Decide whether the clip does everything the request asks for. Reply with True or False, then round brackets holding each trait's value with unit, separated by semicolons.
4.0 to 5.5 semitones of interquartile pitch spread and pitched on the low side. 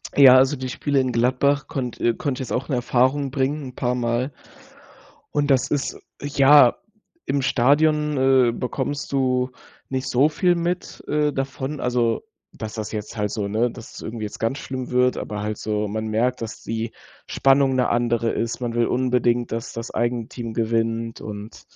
False (2.8 semitones; 125 Hz)